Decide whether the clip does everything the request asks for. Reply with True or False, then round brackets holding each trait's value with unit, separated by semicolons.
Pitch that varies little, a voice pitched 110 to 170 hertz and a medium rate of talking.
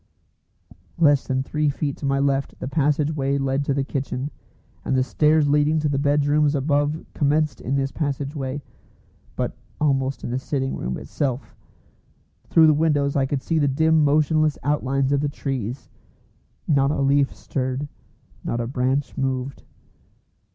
True (1.7 semitones; 140 Hz; 160 wpm)